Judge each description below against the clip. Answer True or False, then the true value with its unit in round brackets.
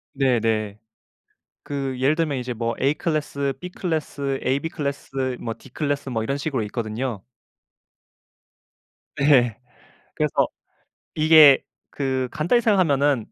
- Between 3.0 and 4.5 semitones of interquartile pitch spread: True (3.3 semitones)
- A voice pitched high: False (135 Hz)